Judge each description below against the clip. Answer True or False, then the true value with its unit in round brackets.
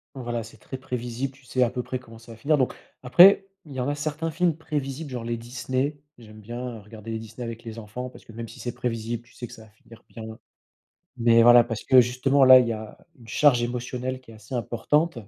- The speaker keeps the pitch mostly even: True (2.3 semitones)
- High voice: False (120 Hz)